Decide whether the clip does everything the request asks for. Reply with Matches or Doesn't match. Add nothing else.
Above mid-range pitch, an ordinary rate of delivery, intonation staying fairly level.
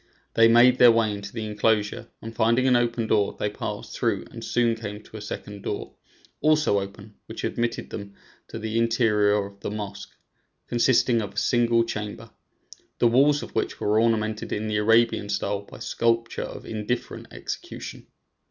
Doesn't match